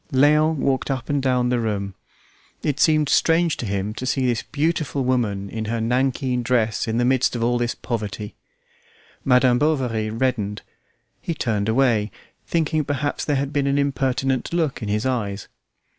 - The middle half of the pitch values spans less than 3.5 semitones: No, average, 3.9 semitones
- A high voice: No, low, 125 Hz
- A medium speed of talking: Yes, average, 170 wpm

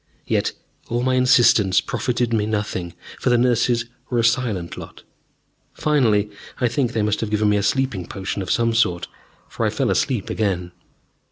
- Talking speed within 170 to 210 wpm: Yes, average, 175 wpm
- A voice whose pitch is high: No, low, 115 Hz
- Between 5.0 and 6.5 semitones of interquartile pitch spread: No, average, 3.1 semitones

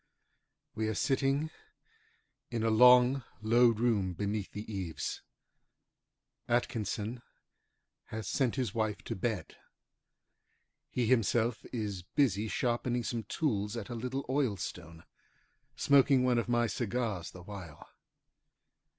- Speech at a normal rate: No, slow, 115 wpm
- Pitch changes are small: No, average, 3.2 semitones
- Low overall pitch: Yes, low, 115 Hz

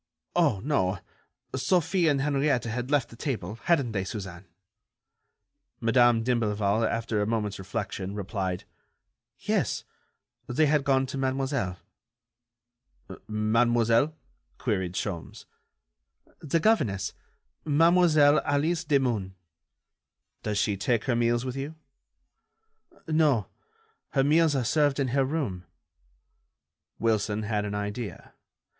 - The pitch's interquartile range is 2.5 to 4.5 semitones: No, wide, 5.5 semitones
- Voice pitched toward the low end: Yes, low, 120 Hz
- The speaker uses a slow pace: Yes, slow, 110 wpm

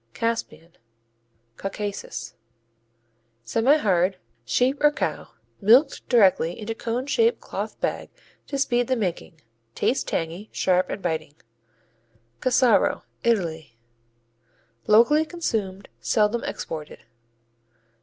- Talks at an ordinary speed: No, slow, 95 wpm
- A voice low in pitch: No, high, 215 Hz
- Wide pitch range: Yes, wide, 5.7 semitones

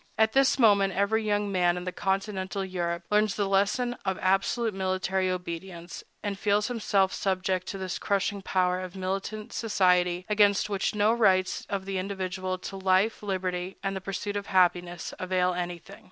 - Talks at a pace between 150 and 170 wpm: Yes, average, 165 wpm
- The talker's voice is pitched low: No, high, 190 Hz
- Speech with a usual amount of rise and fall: No, narrow, 1.8 semitones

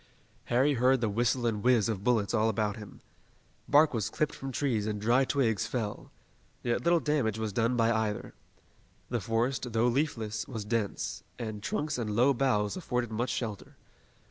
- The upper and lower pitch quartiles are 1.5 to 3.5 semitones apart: Yes, average, 3.1 semitones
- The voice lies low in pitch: Yes, low, 115 Hz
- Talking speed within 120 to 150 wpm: No, average, 170 wpm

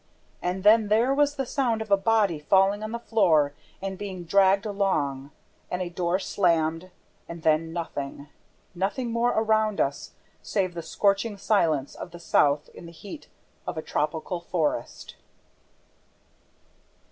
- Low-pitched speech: No, high, 190 Hz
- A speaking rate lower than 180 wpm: Yes, average, 145 wpm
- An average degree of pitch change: Yes, average, 4.6 semitones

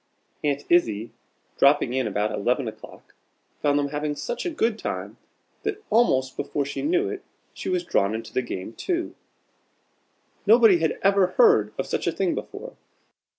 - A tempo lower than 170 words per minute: Yes, average, 160 wpm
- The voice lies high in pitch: No, medium, 150 Hz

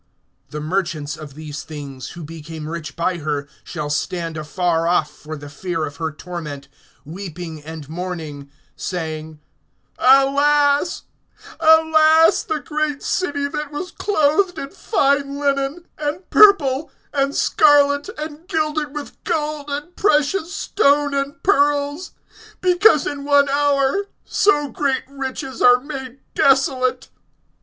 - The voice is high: Yes, very high, 275 Hz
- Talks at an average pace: No, slow, 125 wpm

